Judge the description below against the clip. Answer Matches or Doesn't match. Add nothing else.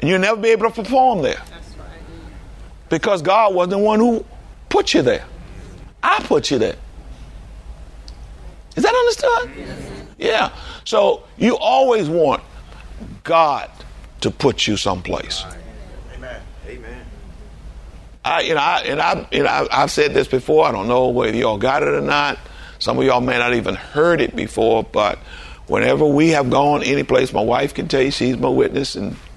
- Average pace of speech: Matches